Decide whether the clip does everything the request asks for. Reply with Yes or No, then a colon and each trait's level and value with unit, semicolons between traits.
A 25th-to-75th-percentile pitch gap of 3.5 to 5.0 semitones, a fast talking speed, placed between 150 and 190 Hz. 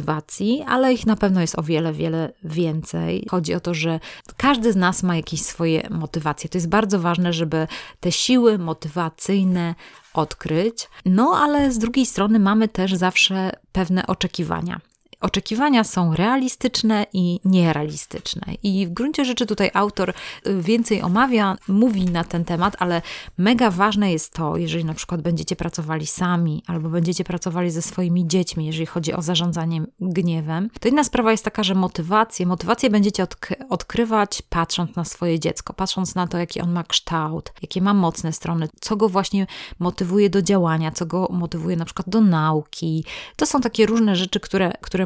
Yes: average, 3.8 semitones; fast, 165 wpm; medium, 185 Hz